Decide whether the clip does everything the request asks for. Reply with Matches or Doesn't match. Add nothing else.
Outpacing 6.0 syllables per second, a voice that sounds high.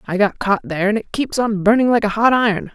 Matches